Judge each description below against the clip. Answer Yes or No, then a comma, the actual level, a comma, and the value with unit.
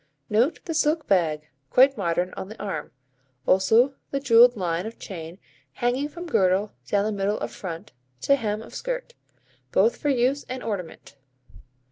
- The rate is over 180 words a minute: No, average, 160 wpm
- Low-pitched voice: No, high, 220 Hz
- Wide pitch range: Yes, wide, 6.7 semitones